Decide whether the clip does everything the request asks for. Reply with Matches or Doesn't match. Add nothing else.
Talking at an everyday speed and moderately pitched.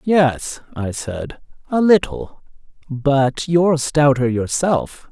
Doesn't match